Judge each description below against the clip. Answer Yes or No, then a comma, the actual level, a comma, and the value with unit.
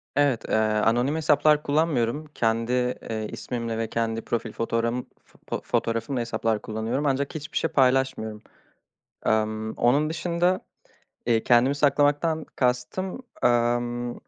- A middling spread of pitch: Yes, average, 4.1 semitones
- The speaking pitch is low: Yes, low, 120 Hz